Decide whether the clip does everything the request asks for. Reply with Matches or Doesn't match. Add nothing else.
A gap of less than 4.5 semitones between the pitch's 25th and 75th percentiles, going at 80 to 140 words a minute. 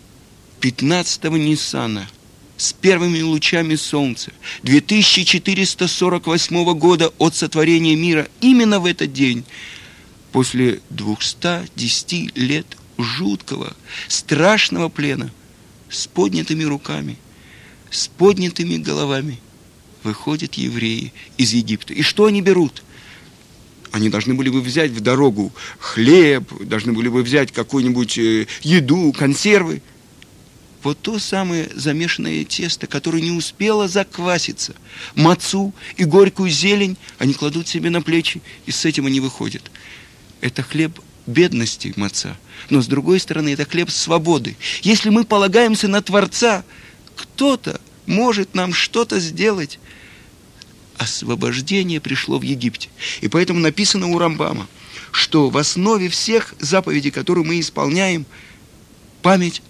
Doesn't match